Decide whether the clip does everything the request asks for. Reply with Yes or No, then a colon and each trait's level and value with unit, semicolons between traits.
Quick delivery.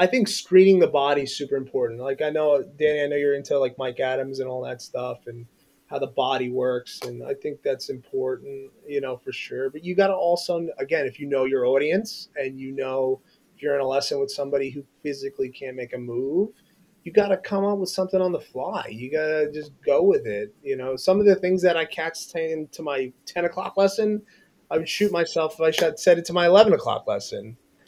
Yes: fast, 225 wpm